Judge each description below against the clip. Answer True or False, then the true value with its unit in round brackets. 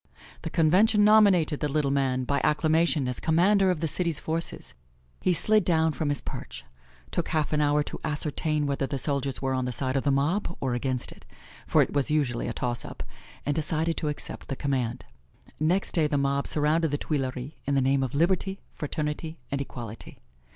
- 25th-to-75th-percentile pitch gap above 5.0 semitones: False (3.1 semitones)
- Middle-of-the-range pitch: True (150 Hz)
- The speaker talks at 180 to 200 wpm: True (195 wpm)